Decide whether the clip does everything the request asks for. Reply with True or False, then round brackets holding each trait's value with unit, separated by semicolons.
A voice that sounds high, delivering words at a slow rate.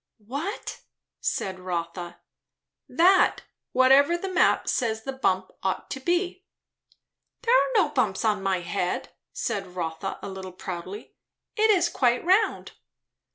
True (235 Hz; 130 wpm)